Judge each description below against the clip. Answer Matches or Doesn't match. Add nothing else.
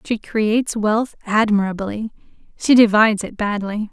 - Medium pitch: Doesn't match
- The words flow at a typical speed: Doesn't match